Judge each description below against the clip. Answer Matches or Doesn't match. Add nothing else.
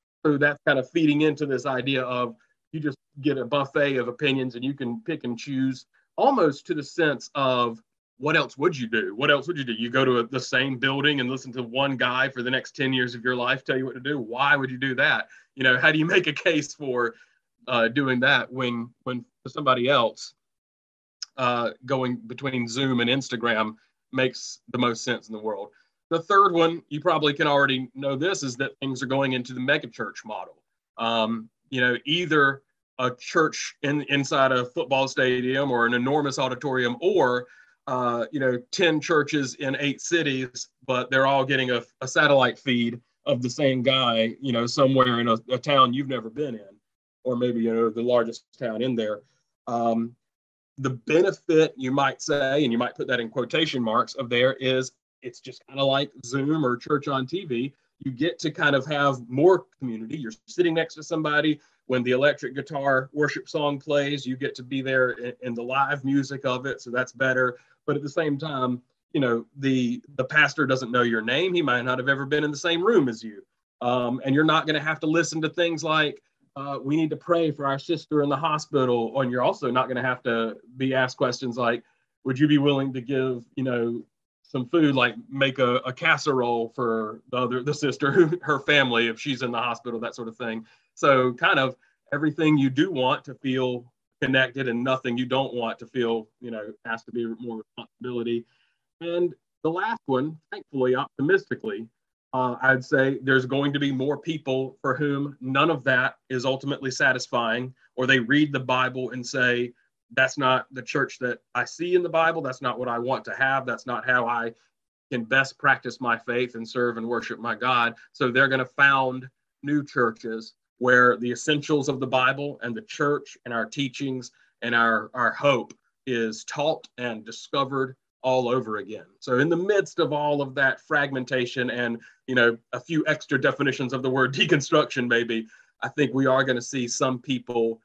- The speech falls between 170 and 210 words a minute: Matches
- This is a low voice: Matches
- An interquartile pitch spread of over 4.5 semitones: Doesn't match